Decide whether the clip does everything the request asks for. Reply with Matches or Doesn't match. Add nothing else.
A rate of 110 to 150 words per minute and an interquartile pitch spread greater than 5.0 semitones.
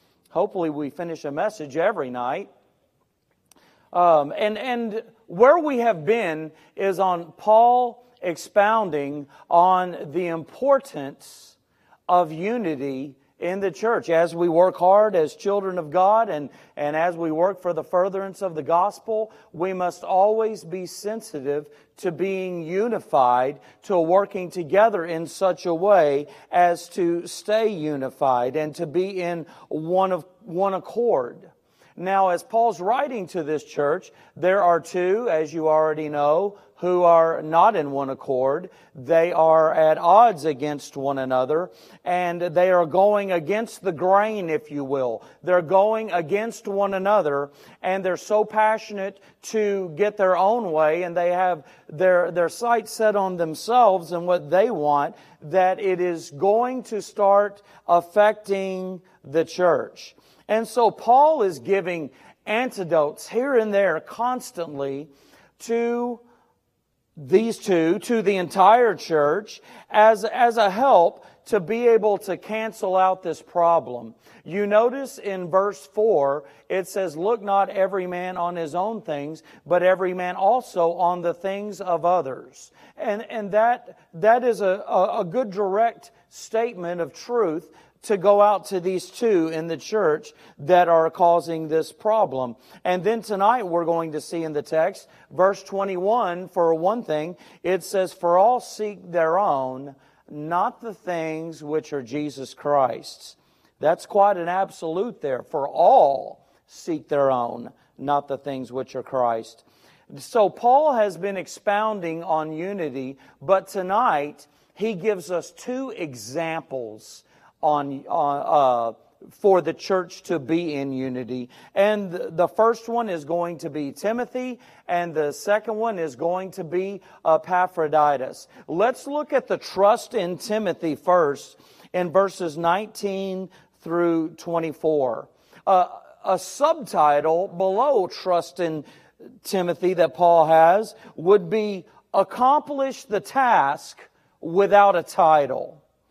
Doesn't match